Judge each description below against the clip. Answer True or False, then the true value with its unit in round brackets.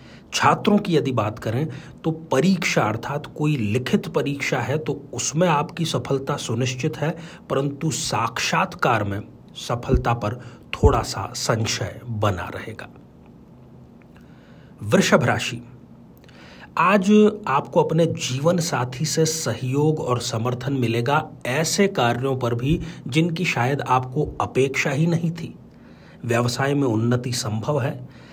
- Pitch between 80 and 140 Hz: True (135 Hz)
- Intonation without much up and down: False (4.8 semitones)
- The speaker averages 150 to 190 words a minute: False (120 wpm)